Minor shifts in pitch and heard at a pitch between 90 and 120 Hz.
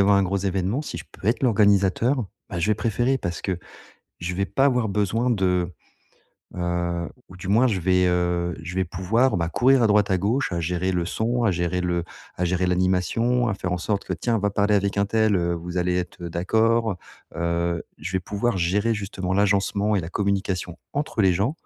No: average, 3.4 semitones; very low, 95 Hz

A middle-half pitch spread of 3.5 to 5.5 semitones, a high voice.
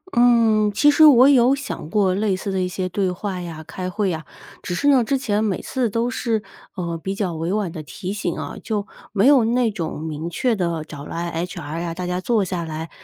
Yes: average, 4.8 semitones; high, 195 Hz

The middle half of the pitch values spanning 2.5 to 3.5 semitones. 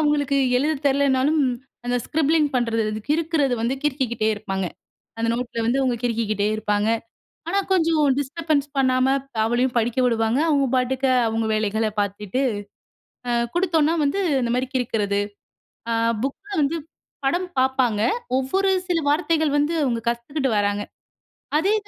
No: average, 4.6 semitones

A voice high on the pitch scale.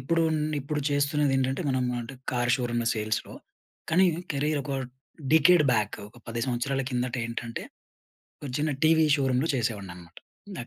No: low, 130 Hz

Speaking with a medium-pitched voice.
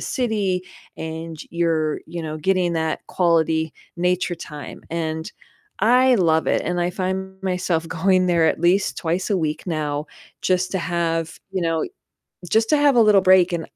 Yes: medium, 175 Hz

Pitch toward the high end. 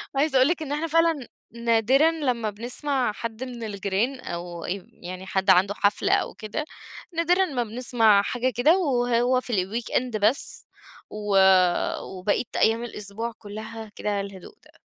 Yes: high, 230 Hz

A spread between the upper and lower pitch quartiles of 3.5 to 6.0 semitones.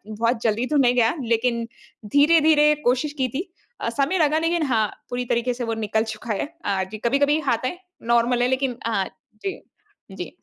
Yes: average, 4.2 semitones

